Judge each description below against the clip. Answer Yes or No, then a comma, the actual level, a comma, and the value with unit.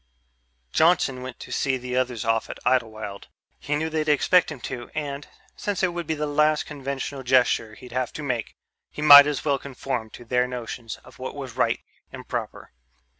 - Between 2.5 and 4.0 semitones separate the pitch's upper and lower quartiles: Yes, average, 3.3 semitones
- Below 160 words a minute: No, average, 190 wpm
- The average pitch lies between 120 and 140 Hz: Yes, low, 135 Hz